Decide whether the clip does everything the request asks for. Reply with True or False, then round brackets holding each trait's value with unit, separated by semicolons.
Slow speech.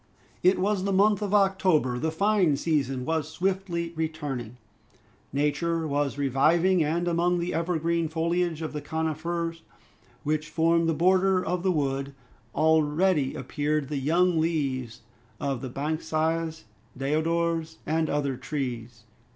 True (130 wpm)